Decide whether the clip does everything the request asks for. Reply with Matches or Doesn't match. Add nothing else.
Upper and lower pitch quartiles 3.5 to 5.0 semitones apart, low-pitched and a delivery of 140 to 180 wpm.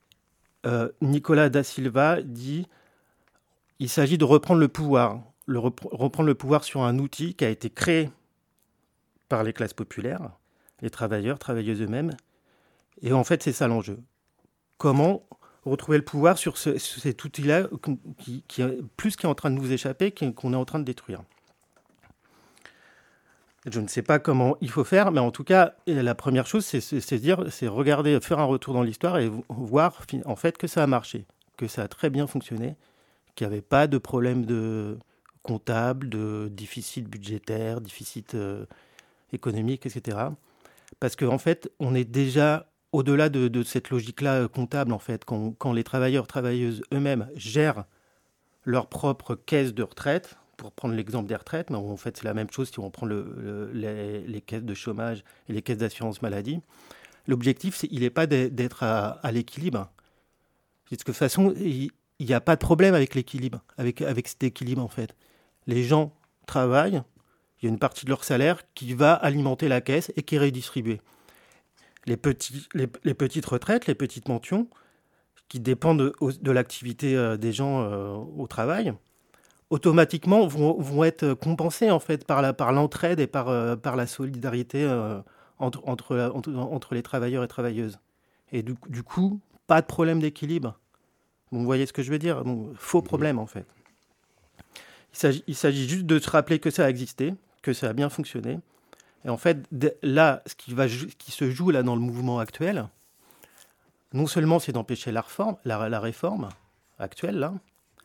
Matches